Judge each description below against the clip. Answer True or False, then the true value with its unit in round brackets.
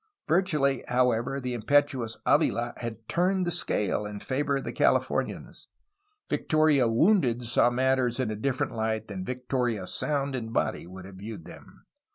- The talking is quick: False (155 wpm)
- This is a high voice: False (125 Hz)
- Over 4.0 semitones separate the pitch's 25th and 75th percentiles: False (3.7 semitones)